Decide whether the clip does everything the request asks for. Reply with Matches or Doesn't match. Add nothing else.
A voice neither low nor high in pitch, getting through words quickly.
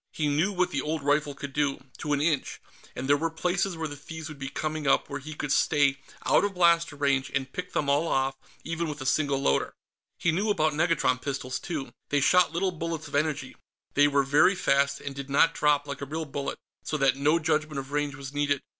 Matches